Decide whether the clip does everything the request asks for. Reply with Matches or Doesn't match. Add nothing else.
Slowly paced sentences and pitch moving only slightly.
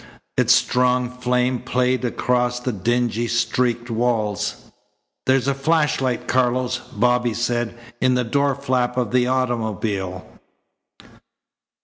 Matches